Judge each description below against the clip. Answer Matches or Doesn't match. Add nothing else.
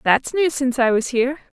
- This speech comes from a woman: Matches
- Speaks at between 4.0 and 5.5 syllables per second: Doesn't match